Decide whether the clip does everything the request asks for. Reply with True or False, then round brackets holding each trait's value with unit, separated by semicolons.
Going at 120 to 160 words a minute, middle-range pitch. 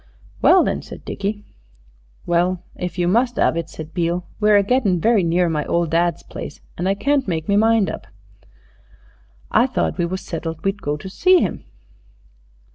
False (180 wpm; 180 Hz)